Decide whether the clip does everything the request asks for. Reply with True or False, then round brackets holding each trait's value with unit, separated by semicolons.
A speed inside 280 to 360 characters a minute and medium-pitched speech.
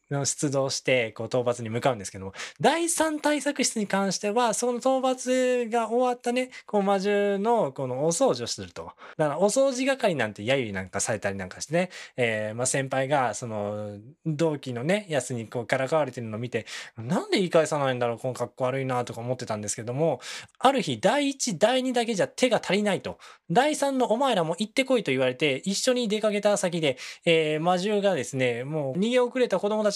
False (400 characters per minute; 165 Hz)